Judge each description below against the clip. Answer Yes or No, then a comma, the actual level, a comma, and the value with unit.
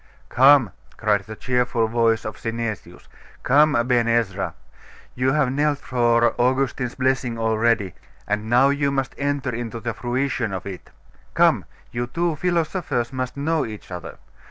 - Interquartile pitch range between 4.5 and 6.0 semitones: No, average, 3.3 semitones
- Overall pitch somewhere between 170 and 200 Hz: No, low, 120 Hz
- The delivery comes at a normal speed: Yes, average, 145 wpm